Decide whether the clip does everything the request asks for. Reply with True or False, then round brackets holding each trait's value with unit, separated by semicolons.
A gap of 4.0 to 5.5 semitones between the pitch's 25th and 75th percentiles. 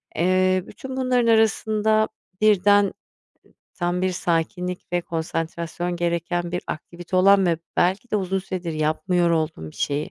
False (2.8 semitones)